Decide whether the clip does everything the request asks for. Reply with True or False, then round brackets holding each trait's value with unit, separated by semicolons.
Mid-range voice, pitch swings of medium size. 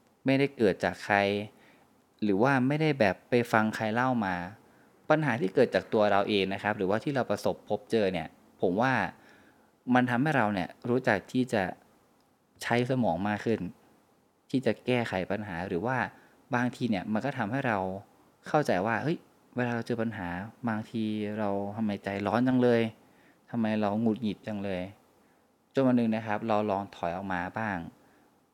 False (110 Hz; 3.4 semitones)